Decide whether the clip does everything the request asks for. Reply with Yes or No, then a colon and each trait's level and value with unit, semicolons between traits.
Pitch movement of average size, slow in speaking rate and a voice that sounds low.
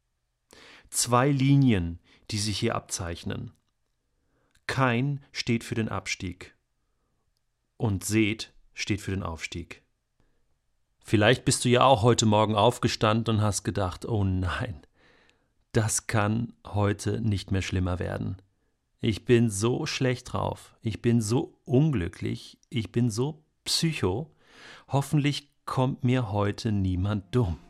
Yes: average, 4.1 semitones; slow, 120 wpm; low, 110 Hz